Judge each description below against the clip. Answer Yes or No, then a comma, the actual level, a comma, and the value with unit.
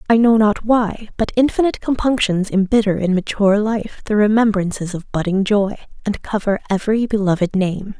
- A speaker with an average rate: Yes, average, 160 wpm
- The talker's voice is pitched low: No, high, 210 Hz